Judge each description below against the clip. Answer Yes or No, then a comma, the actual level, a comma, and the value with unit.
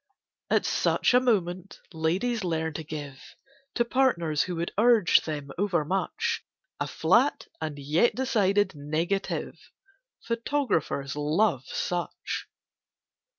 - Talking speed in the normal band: No, slow, 110 wpm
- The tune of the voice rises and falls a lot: Yes, wide, 6.0 semitones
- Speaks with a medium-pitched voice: Yes, medium, 175 Hz